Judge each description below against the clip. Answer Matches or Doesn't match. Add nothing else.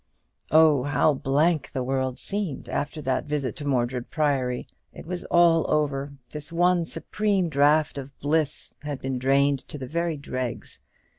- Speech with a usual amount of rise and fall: Matches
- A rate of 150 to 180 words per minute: Matches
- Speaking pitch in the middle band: Matches